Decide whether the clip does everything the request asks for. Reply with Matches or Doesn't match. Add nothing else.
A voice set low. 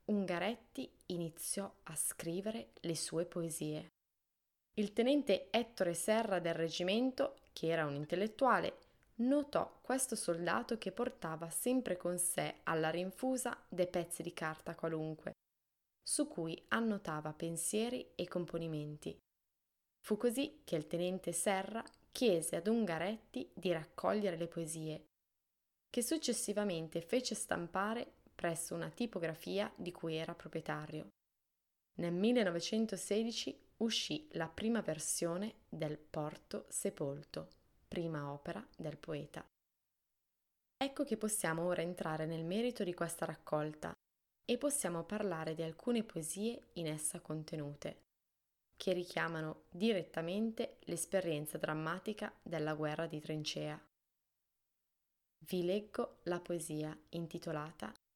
Doesn't match